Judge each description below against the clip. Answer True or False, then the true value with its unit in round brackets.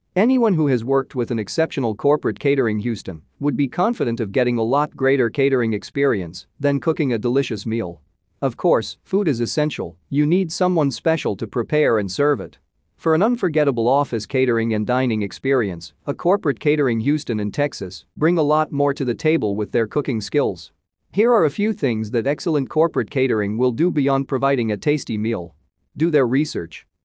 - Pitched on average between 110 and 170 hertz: True (135 Hz)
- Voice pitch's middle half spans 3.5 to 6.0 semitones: True (4.8 semitones)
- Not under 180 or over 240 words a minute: True (185 wpm)